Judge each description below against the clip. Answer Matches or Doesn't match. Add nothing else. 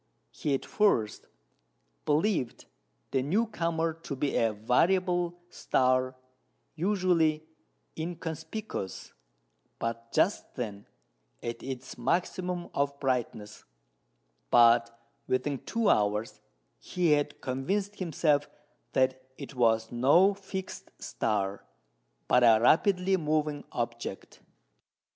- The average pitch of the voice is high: Doesn't match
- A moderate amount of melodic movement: Doesn't match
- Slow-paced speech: Matches